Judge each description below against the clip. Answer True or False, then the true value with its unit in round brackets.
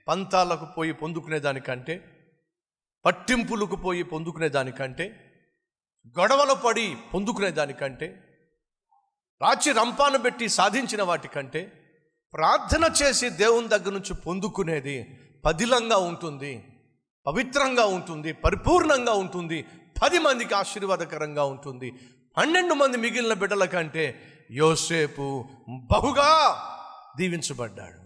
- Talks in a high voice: False (170 Hz)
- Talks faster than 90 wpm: False (85 wpm)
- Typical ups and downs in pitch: False (6.9 semitones)